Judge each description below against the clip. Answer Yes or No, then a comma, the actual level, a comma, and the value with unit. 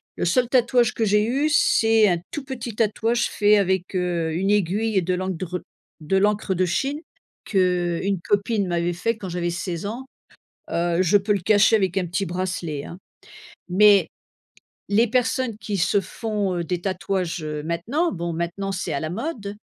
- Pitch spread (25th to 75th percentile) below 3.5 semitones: No, average, 3.8 semitones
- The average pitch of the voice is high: Yes, high, 195 Hz